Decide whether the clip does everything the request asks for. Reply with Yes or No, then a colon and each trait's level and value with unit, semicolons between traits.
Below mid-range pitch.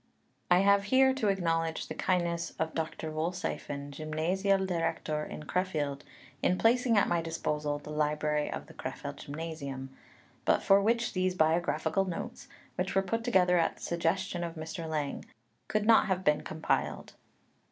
No: medium, 170 Hz